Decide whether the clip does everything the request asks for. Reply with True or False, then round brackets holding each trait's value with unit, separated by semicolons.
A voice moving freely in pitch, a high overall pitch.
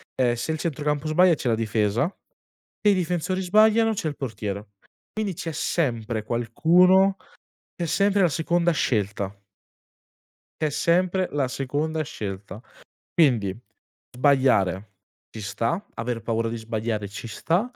False (7.5 semitones; 140 Hz)